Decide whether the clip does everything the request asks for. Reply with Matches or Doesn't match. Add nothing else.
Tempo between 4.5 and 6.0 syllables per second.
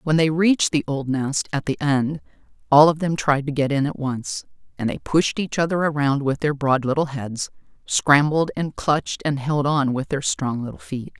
Matches